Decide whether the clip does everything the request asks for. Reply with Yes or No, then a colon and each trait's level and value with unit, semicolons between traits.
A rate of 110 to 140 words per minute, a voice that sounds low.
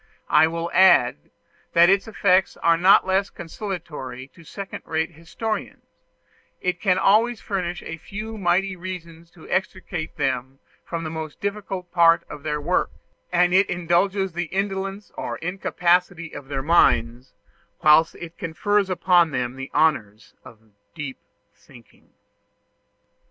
No: slow, 135 wpm; medium, 170 Hz